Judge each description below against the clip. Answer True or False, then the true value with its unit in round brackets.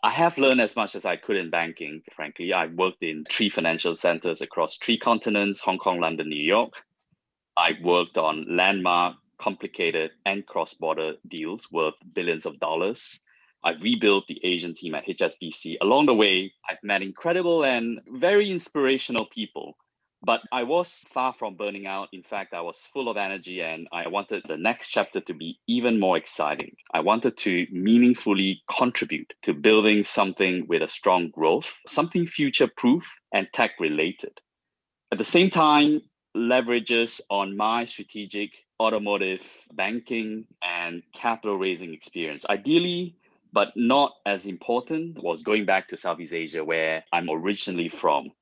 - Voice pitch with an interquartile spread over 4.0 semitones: True (5.0 semitones)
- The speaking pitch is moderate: False (105 Hz)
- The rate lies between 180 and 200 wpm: False (155 wpm)